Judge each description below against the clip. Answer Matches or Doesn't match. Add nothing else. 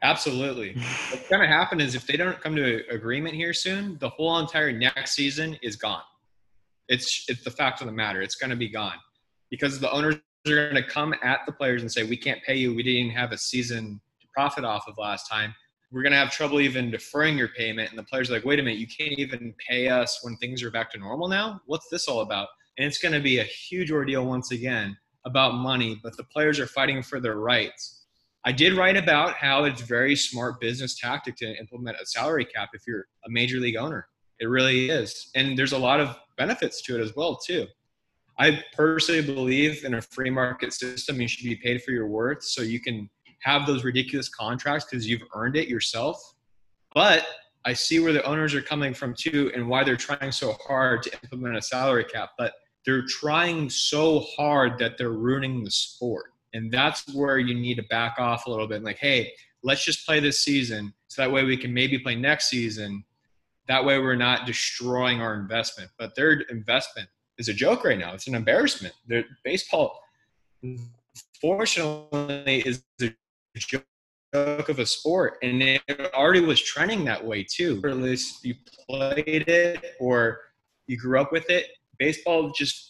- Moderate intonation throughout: Matches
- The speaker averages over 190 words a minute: Matches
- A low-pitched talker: Matches